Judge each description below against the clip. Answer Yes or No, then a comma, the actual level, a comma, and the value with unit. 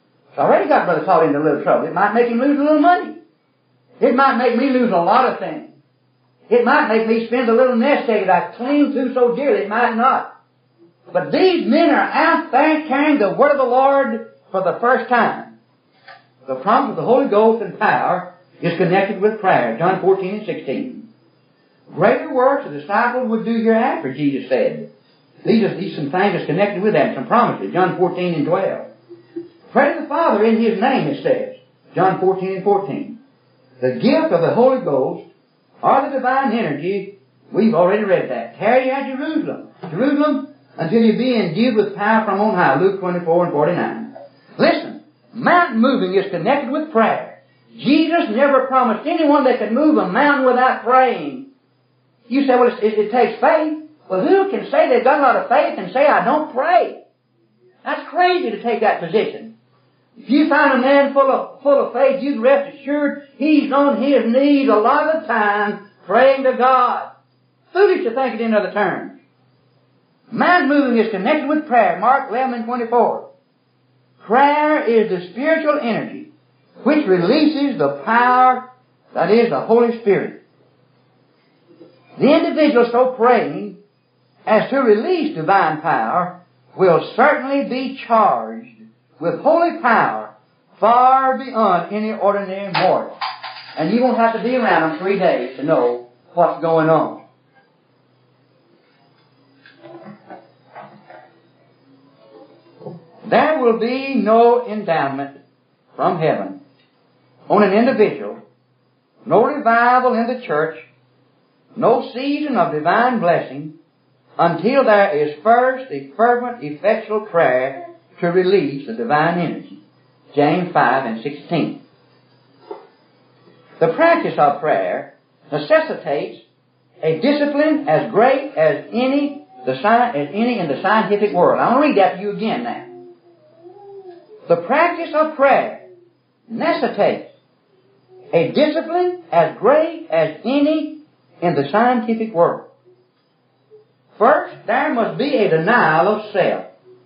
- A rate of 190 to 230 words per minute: No, average, 150 wpm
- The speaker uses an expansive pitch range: Yes, wide, 7.0 semitones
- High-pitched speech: Yes, high, 235 Hz